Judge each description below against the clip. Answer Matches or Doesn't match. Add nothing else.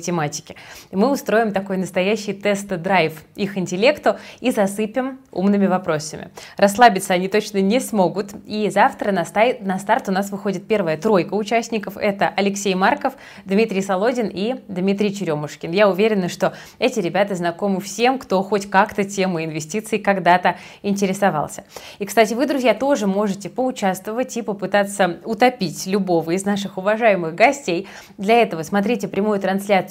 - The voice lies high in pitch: Matches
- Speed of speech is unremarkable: Matches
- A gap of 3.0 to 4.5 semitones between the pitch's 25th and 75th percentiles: Doesn't match